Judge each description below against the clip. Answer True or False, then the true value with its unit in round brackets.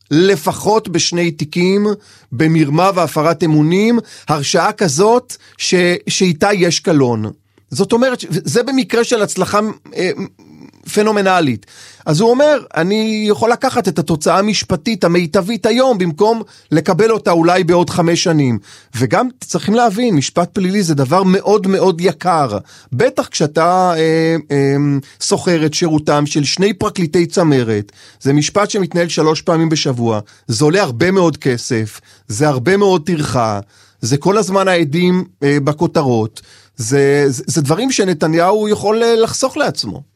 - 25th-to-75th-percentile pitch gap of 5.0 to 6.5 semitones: True (5.4 semitones)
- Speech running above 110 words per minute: True (130 wpm)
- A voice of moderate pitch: True (175 Hz)